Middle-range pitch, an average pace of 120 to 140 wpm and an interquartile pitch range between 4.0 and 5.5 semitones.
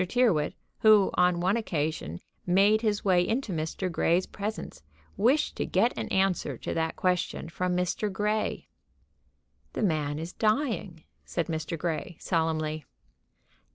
Yes: medium, 180 Hz; slow, 135 wpm; average, 4.5 semitones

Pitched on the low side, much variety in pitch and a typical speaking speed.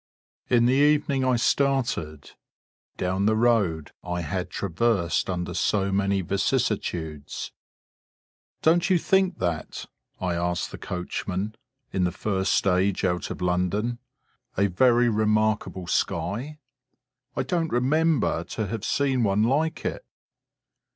No: low, 105 Hz; wide, 5.8 semitones; slow, 125 wpm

